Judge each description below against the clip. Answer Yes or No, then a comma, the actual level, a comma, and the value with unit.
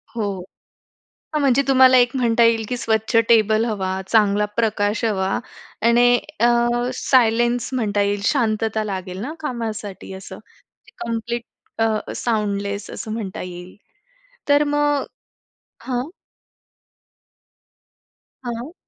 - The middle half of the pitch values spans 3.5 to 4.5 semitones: No, average, 2.8 semitones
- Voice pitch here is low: No, high, 225 Hz